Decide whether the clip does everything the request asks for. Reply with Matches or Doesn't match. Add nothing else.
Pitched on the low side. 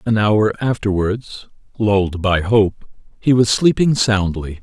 Matches